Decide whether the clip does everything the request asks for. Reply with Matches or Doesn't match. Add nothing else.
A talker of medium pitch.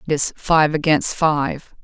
Matches